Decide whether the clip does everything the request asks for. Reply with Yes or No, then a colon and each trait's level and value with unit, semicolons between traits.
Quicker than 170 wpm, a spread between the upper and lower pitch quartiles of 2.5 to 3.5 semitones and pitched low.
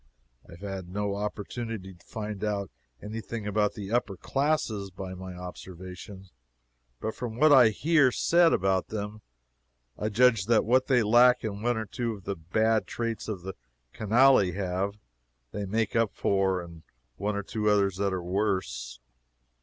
No: average, 165 wpm; average, 3.0 semitones; low, 105 Hz